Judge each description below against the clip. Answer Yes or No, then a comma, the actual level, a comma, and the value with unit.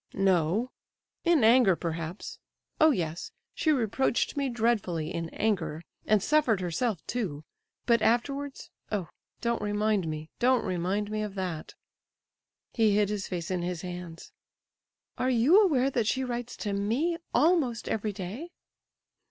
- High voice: Yes, high, 215 Hz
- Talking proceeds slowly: Yes, slow, 130 wpm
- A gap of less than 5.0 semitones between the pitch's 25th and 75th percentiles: No, wide, 5.6 semitones